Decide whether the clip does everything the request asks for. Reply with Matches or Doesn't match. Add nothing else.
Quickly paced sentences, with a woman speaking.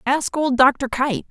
Doesn't match